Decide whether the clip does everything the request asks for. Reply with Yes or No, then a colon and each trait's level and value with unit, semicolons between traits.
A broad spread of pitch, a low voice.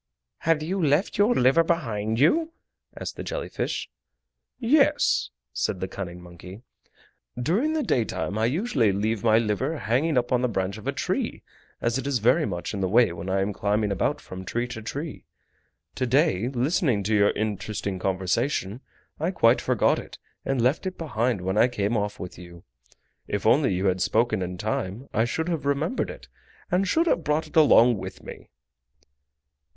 Yes: wide, 7.3 semitones; low, 120 Hz